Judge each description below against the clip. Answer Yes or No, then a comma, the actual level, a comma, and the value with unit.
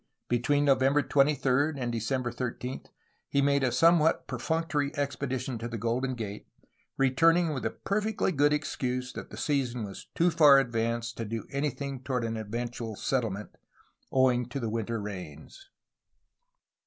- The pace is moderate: Yes, average, 150 wpm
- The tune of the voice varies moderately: Yes, average, 3.5 semitones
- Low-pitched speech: Yes, low, 130 Hz